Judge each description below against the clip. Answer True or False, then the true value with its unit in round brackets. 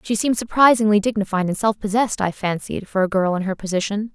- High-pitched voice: True (205 Hz)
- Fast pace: True (215 wpm)